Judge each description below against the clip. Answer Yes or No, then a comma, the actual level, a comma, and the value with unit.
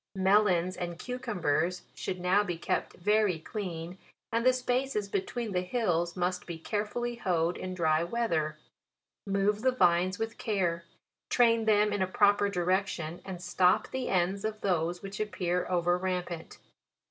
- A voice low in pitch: No, medium, 185 Hz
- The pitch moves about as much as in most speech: Yes, average, 3.4 semitones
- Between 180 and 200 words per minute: No, average, 155 wpm